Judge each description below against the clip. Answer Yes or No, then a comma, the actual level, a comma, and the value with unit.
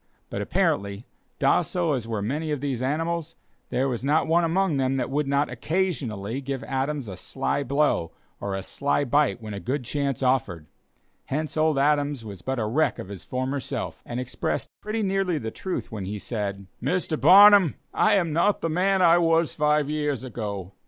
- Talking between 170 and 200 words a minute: Yes, average, 185 wpm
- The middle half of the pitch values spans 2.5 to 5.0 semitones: No, wide, 5.4 semitones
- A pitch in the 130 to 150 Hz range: Yes, medium, 140 Hz